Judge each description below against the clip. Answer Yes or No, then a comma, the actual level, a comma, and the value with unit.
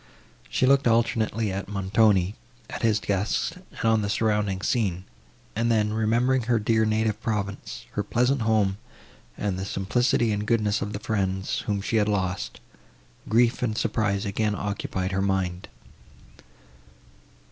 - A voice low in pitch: Yes, low, 105 Hz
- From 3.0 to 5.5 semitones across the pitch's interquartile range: No, narrow, 2.4 semitones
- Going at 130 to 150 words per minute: Yes, average, 145 wpm